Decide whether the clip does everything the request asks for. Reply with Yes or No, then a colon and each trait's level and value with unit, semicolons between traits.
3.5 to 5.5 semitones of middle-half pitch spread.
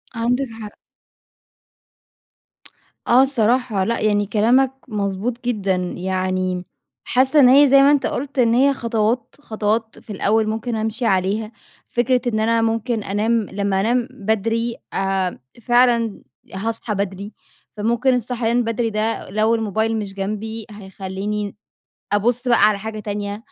No: average, 2.8 semitones